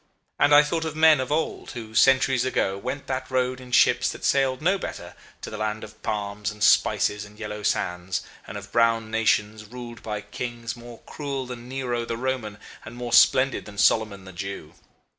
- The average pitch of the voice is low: Yes, low, 115 Hz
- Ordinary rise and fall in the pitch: Yes, average, 3.7 semitones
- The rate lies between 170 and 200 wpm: Yes, average, 195 wpm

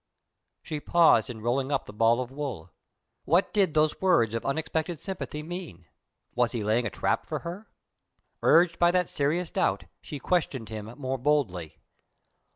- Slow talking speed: No, average, 165 wpm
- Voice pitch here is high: No, medium, 140 Hz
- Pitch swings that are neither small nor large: No, wide, 6.7 semitones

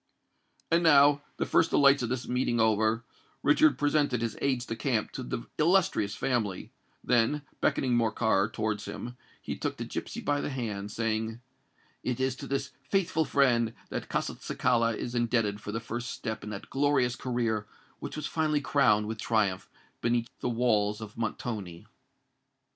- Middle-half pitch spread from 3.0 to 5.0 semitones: Yes, average, 4.0 semitones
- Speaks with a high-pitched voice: No, low, 120 Hz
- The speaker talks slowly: No, average, 160 wpm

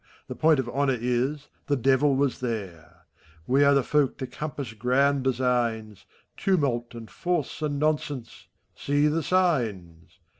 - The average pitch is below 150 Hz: Yes, low, 135 Hz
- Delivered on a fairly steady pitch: No, average, 3.7 semitones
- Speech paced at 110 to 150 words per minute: Yes, average, 145 wpm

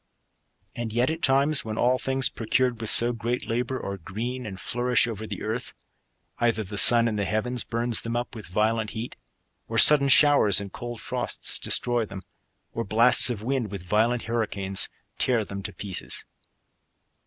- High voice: No, low, 115 Hz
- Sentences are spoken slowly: No, average, 175 wpm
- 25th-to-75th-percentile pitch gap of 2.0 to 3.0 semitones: Yes, narrow, 2.6 semitones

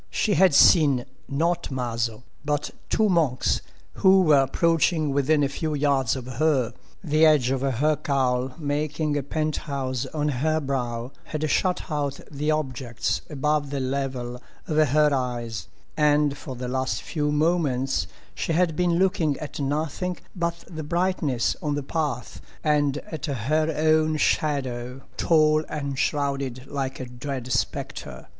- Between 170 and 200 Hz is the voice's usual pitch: No, medium, 145 Hz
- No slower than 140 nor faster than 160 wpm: Yes, average, 145 wpm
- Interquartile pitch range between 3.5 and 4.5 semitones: No, average, 3.0 semitones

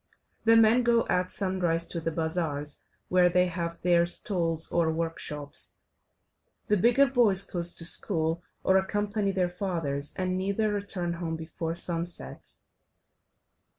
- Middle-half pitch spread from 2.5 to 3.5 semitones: Yes, average, 3.1 semitones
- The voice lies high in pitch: No, medium, 175 Hz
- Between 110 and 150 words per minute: Yes, slow, 135 wpm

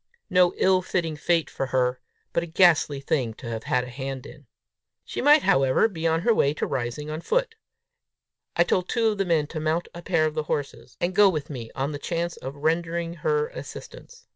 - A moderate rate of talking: No, fast, 210 wpm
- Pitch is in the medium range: Yes, medium, 160 Hz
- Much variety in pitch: No, average, 4.5 semitones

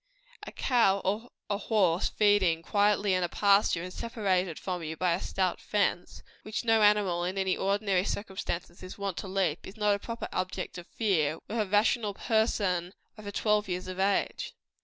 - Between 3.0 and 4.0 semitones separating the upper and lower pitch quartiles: No, narrow, 2.4 semitones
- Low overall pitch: No, high, 195 Hz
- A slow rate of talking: No, average, 180 wpm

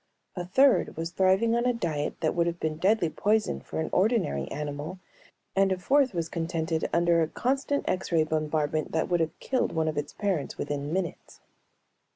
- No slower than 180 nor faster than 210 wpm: Yes, average, 190 wpm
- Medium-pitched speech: Yes, medium, 170 Hz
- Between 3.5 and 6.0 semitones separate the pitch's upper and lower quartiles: Yes, average, 4.0 semitones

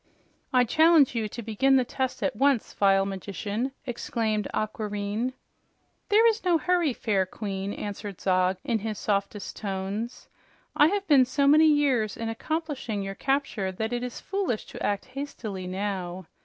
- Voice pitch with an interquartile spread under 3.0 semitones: No, wide, 5.5 semitones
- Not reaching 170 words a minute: Yes, average, 155 wpm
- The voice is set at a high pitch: Yes, high, 225 Hz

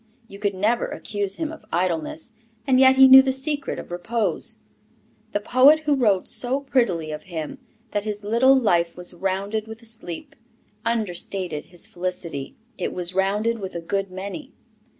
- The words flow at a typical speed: Yes, average, 170 wpm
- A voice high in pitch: Yes, high, 205 Hz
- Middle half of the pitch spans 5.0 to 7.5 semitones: Yes, wide, 5.6 semitones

